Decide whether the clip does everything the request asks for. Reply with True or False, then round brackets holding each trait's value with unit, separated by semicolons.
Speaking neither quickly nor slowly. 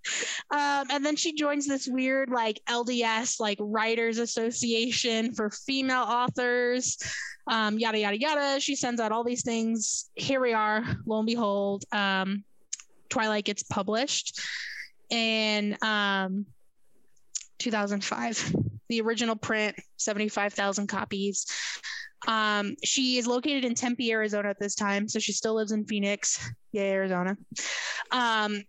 False (130 wpm)